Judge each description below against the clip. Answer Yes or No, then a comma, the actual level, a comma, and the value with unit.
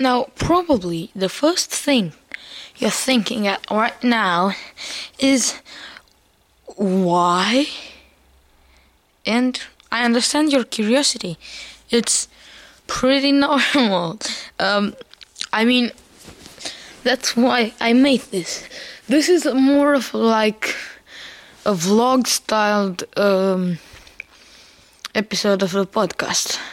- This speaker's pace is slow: Yes, slow, 90 wpm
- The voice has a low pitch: No, high, 230 Hz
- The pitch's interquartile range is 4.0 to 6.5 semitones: Yes, average, 5.1 semitones